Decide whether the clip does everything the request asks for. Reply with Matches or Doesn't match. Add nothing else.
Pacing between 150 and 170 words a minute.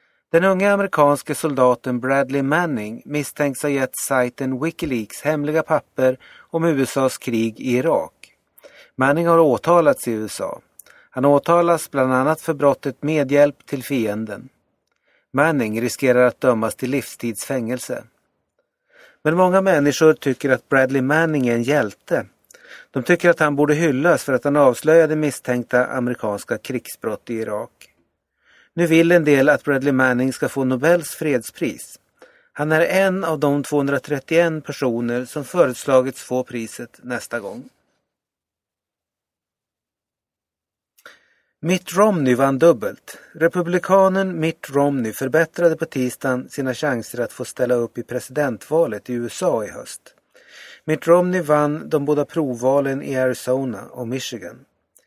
Doesn't match